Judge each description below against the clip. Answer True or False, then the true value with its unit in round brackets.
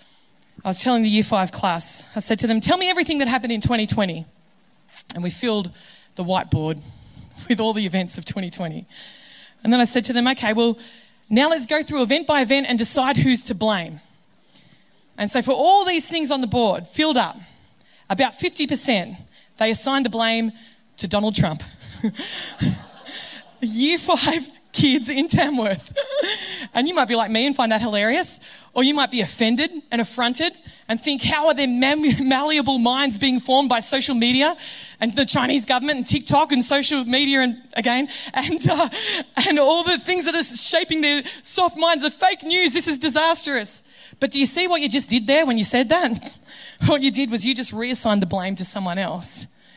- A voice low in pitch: False (250 Hz)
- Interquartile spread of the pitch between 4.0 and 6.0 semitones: True (4.8 semitones)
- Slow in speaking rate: False (190 wpm)